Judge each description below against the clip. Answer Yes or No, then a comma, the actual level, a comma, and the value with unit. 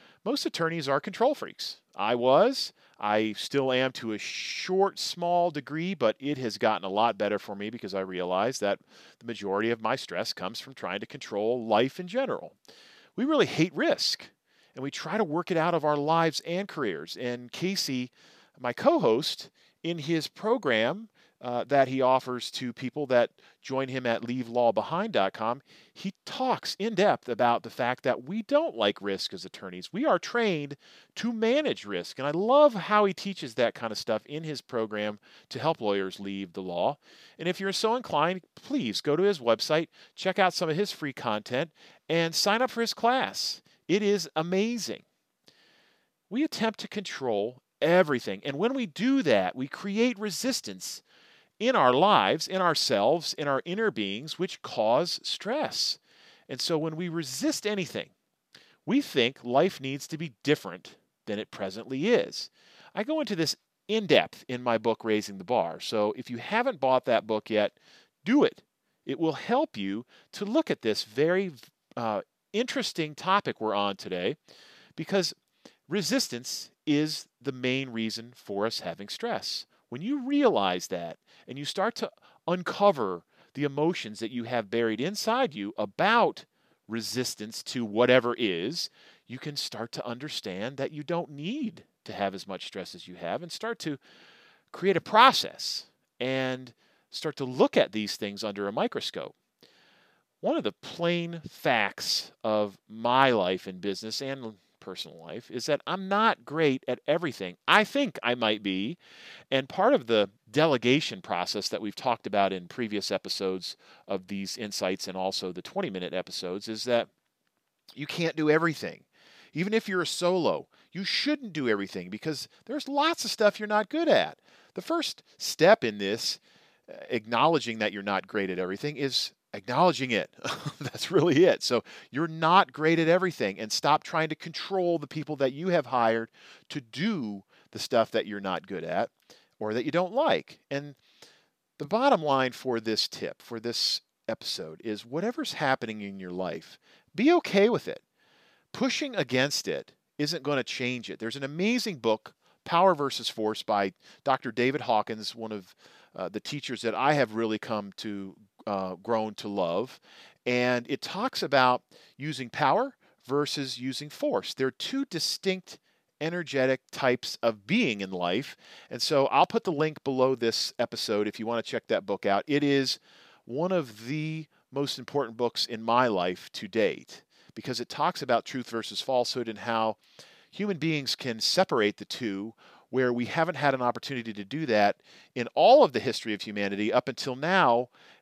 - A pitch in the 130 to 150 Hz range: Yes, medium, 140 Hz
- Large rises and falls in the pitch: Yes, wide, 8.1 semitones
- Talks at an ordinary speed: Yes, average, 170 wpm